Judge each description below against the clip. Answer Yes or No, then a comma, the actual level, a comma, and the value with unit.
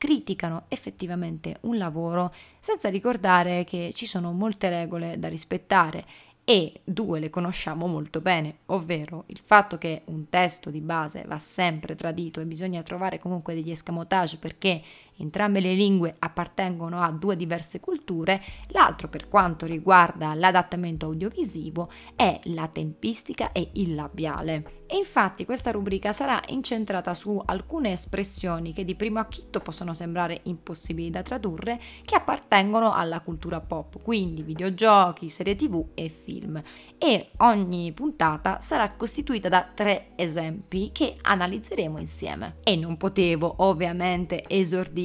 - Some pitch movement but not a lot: Yes, average, 3.3 semitones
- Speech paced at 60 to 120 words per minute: No, average, 135 wpm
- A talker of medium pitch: Yes, medium, 180 Hz